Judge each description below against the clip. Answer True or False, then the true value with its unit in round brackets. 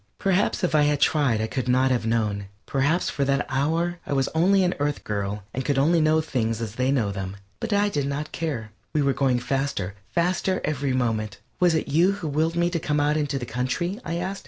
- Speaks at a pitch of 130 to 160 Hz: True (140 Hz)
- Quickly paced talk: True (230 wpm)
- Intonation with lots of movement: False (4.9 semitones)